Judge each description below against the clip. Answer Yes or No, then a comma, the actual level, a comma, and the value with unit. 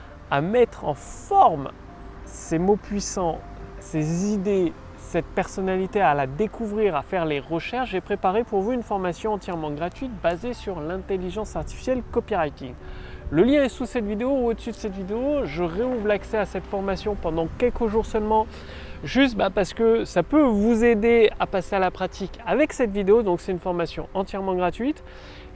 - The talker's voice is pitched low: No, high, 205 Hz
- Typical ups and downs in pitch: Yes, average, 4.2 semitones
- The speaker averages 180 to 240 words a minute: No, average, 170 wpm